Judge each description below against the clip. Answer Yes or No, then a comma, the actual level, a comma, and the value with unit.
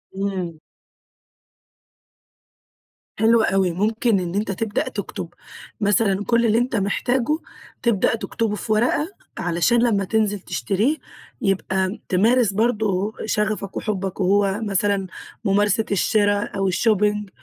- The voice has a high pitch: Yes, high, 205 Hz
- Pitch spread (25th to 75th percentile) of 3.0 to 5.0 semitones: No, narrow, 2.4 semitones